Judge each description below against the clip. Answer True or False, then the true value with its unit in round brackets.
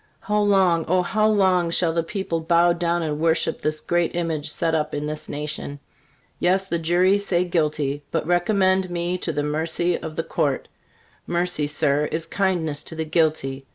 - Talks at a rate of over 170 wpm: True (180 wpm)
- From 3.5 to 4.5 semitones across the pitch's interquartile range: False (2.8 semitones)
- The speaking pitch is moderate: True (170 Hz)